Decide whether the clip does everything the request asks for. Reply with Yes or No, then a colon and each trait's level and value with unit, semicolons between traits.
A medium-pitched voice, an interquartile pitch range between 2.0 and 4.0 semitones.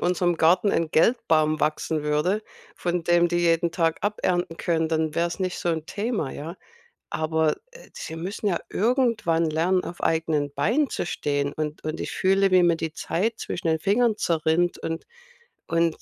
Yes: medium, 170 Hz; average, 2.7 semitones